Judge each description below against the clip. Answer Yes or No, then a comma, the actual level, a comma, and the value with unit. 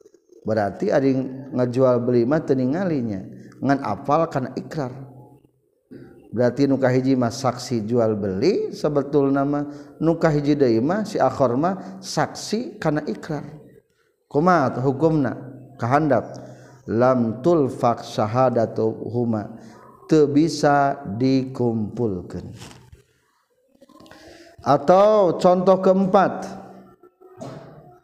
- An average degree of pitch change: Yes, average, 4.5 semitones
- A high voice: No, medium, 140 Hz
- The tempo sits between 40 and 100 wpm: Yes, average, 90 wpm